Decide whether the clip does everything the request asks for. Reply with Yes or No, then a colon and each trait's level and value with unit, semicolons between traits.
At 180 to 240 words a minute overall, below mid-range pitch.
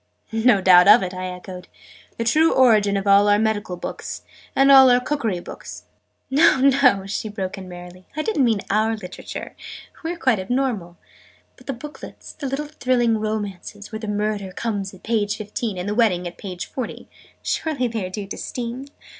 No: average, 190 wpm; high, 215 Hz